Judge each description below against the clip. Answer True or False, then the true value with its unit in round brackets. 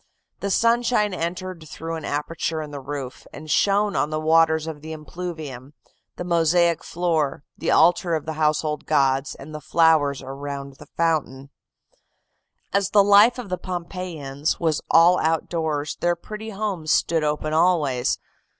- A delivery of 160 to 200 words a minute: False (150 wpm)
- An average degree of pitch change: True (3.1 semitones)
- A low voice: False (160 Hz)